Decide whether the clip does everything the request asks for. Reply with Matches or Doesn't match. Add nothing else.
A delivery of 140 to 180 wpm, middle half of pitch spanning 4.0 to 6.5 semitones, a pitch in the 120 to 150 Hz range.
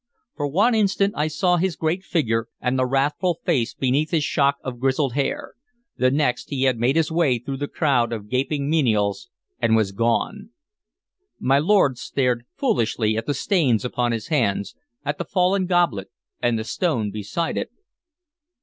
Matches